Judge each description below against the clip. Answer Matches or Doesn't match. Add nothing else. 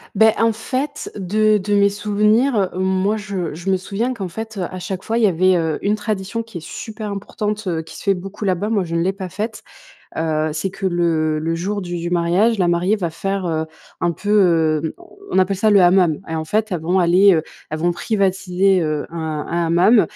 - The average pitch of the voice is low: Doesn't match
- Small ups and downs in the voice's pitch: Doesn't match